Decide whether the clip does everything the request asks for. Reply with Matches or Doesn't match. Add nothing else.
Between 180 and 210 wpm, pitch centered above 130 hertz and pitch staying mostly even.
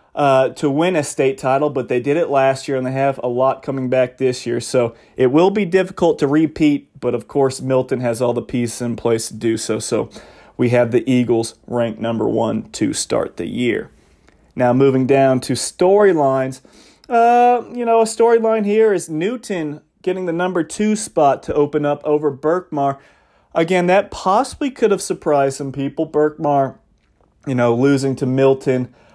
Doesn't match